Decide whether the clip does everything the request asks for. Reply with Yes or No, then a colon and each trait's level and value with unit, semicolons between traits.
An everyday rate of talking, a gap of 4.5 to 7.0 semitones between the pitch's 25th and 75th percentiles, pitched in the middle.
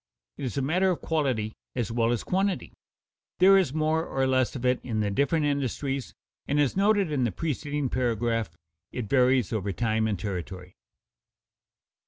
No: average, 170 wpm; average, 5.0 semitones; low, 130 Hz